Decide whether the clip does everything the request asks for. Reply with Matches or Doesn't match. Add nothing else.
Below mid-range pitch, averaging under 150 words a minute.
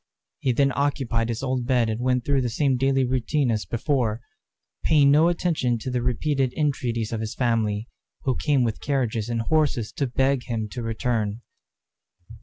Doesn't match